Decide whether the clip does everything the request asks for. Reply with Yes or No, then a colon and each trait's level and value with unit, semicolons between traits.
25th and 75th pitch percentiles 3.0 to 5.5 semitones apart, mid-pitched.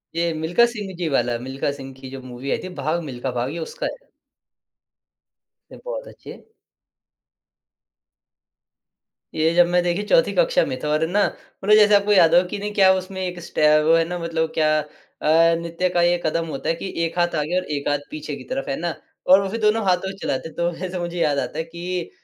Yes: average, 3.7 semitones; medium, 170 Hz